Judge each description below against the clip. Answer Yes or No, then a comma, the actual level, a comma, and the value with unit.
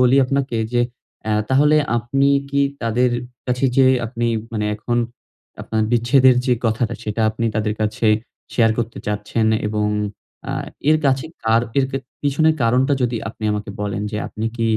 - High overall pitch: No, low, 120 Hz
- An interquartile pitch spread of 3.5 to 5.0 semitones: No, average, 3.1 semitones